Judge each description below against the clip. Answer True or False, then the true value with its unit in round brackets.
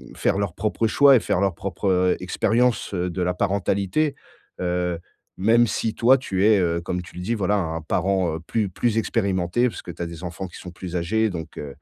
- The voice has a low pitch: True (95 Hz)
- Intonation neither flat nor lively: True (3.7 semitones)